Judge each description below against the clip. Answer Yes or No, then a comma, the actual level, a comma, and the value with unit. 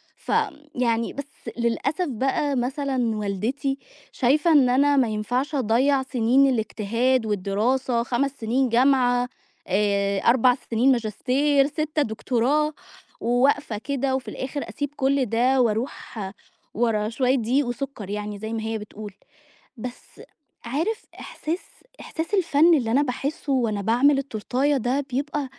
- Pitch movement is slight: No, average, 3.7 semitones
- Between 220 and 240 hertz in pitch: No, very high, 255 Hz